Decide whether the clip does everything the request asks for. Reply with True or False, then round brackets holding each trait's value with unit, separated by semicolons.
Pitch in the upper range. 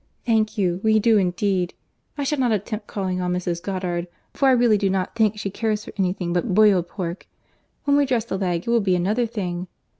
True (200 Hz)